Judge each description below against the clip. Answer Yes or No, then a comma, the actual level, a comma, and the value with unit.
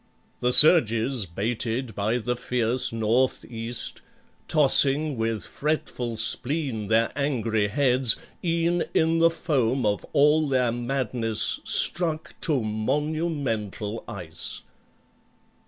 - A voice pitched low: Yes, low, 125 Hz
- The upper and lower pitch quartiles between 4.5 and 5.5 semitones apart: Yes, average, 4.8 semitones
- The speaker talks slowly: Yes, slow, 105 wpm